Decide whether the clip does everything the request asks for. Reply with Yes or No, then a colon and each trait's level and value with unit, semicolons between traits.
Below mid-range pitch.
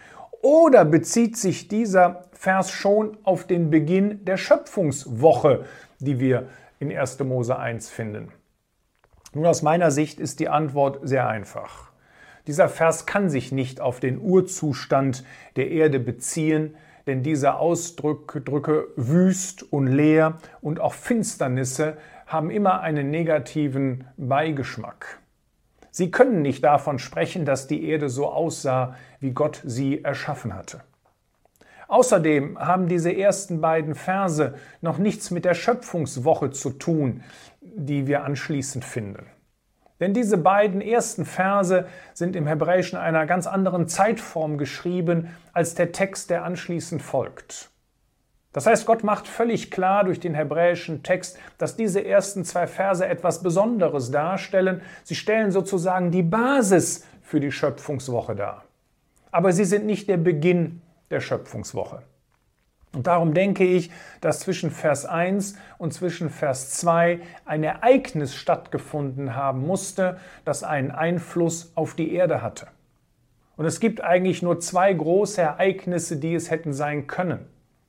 No: medium, 165 Hz